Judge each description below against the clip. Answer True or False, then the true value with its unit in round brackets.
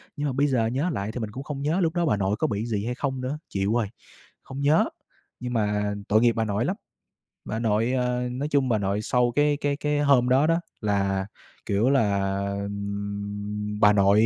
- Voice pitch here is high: False (115 Hz)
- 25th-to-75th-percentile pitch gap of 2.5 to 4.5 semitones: False (5.1 semitones)